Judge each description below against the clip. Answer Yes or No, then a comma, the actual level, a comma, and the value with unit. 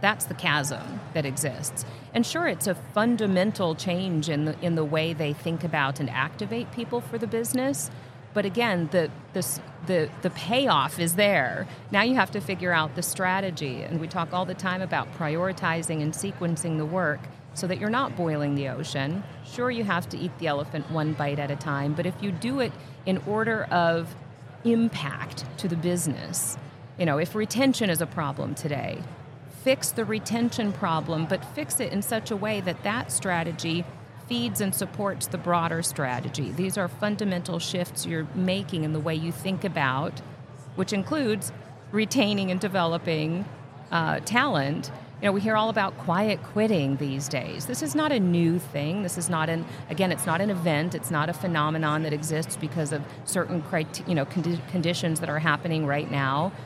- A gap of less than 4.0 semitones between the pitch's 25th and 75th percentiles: No, average, 4.5 semitones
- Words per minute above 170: Yes, average, 185 wpm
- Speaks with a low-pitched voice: No, medium, 165 Hz